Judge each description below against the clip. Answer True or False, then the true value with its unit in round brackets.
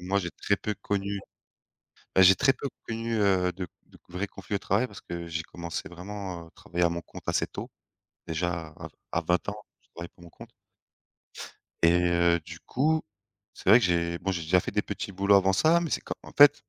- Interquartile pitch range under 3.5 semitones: True (2.9 semitones)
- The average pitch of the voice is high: False (95 Hz)